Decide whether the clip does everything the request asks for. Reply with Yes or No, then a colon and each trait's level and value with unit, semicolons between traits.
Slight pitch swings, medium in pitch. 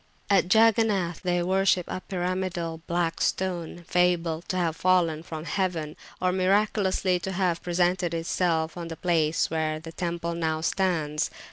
Yes: narrow, 2.1 semitones; medium, 175 Hz